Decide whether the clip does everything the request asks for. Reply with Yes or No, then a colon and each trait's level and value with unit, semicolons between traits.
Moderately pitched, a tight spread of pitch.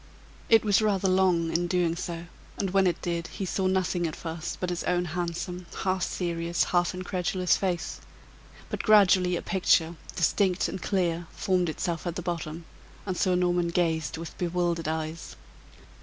Yes: medium, 175 Hz; narrow, 1.6 semitones